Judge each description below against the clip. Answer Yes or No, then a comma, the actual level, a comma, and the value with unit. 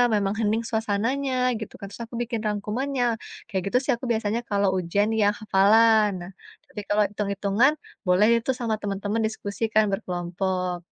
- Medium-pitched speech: No, high, 210 Hz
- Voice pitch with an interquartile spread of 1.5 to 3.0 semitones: Yes, narrow, 2.4 semitones